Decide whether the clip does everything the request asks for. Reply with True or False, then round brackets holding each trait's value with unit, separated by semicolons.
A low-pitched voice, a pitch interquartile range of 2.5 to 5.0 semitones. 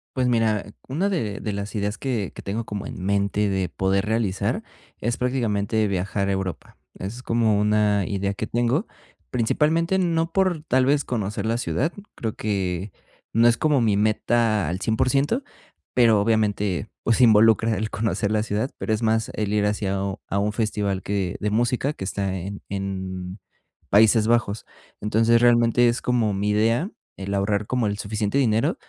True (110 Hz; 2.9 semitones)